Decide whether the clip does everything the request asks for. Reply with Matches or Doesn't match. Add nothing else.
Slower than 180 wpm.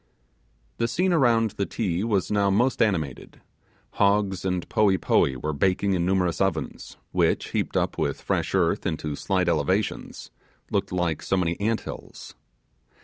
Matches